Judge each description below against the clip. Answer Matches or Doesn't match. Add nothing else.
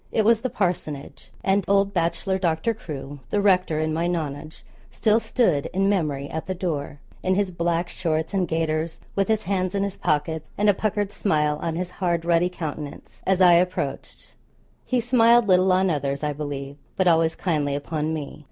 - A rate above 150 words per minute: Matches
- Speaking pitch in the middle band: Matches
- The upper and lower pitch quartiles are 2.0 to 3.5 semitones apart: Doesn't match